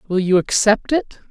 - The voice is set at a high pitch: Yes, high, 210 Hz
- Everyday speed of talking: Yes, average, 185 wpm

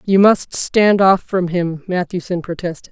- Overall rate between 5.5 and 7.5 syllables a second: No, 4.3 syllables/s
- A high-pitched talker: No, medium, 180 Hz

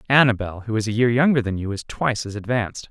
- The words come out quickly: Yes, fast, 250 wpm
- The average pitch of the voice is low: Yes, low, 115 Hz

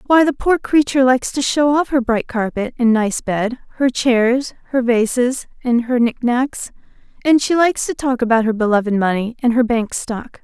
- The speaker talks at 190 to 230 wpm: Yes, average, 200 wpm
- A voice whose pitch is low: No, high, 245 Hz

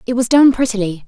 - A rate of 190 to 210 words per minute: No, fast, 225 wpm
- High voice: Yes, high, 230 Hz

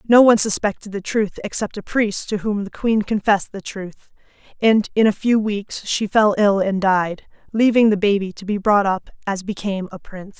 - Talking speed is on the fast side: Yes, fast, 210 wpm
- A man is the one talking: No, female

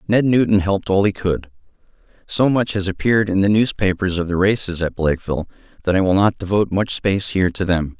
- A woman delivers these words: No, male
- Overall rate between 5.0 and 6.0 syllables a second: No, 6.3 syllables/s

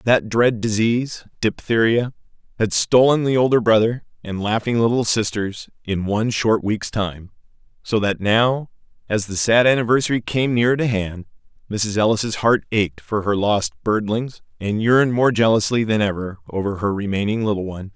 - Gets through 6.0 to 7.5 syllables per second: No, 4.9 syllables/s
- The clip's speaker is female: No, male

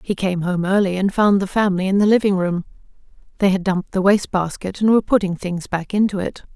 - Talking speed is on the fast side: Yes, fast, 220 wpm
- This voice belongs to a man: No, female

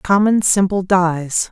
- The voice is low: No, medium, 185 Hz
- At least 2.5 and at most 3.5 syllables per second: Yes, 3.4 syllables/s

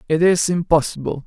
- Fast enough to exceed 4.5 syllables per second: Yes, 5.5 syllables/s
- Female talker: No, male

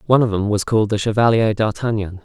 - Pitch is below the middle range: Yes, low, 110 Hz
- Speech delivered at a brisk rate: Yes, fast, 215 wpm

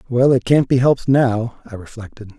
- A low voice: Yes, low, 120 Hz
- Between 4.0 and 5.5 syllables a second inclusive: Yes, 5.3 syllables/s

